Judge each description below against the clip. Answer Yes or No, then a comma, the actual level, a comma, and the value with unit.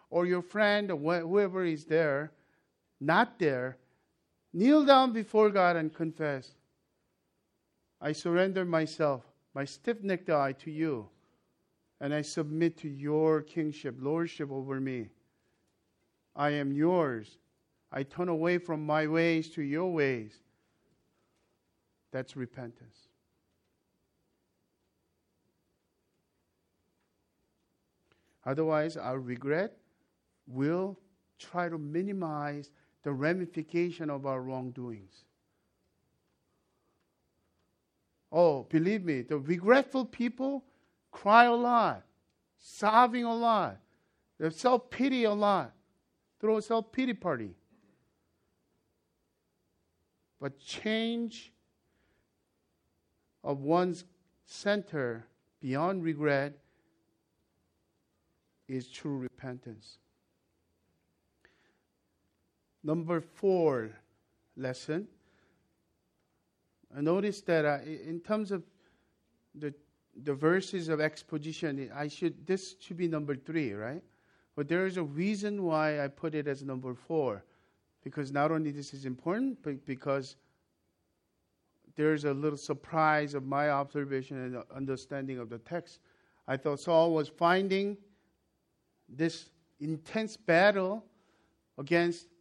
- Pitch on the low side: No, medium, 155 Hz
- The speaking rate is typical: No, slow, 100 wpm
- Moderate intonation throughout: Yes, average, 4.9 semitones